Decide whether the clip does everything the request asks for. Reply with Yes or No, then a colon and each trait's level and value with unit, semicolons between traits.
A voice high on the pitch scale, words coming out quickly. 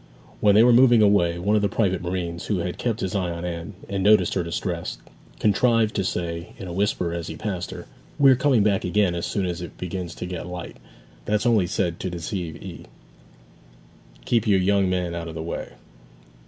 No: very low, 95 Hz; fast, 210 wpm